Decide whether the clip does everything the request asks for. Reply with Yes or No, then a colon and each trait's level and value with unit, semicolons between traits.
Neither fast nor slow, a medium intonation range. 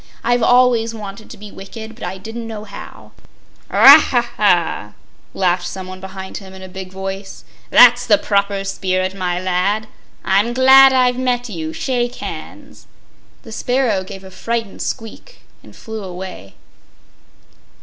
Yes: average, 150 wpm; average, 3.9 semitones